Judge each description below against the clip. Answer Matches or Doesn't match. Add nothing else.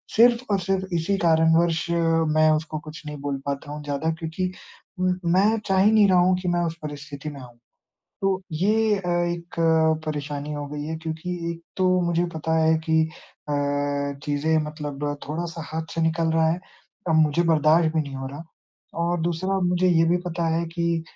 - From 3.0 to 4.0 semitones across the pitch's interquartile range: Doesn't match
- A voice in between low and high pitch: Matches